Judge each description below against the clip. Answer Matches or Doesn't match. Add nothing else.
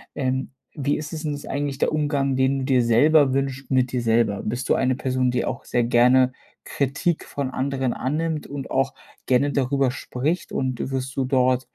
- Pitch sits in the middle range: Doesn't match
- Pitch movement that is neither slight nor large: Doesn't match